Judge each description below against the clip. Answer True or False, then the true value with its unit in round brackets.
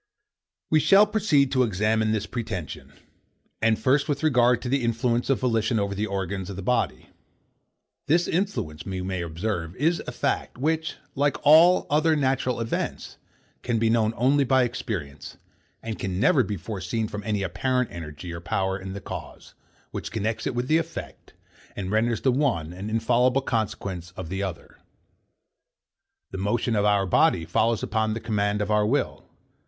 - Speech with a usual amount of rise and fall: True (4.9 semitones)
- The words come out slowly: False (170 wpm)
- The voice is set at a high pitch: False (110 Hz)